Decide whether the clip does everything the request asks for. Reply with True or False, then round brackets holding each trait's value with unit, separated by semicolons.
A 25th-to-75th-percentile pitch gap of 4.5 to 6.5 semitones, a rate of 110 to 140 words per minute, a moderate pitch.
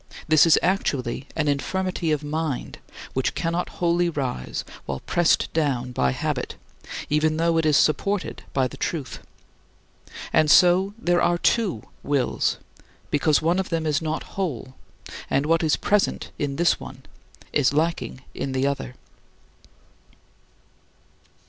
False (3.8 semitones; 135 wpm; 155 Hz)